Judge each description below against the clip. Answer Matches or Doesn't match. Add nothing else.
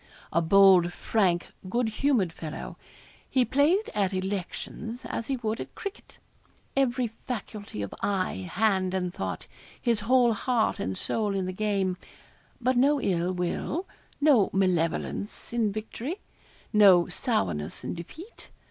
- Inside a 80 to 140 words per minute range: Matches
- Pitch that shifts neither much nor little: Matches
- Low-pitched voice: Doesn't match